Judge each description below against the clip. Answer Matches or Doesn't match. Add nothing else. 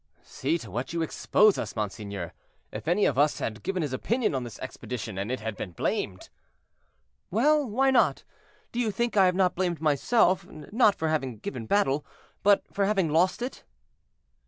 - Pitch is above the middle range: Doesn't match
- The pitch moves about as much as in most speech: Doesn't match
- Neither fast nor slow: Matches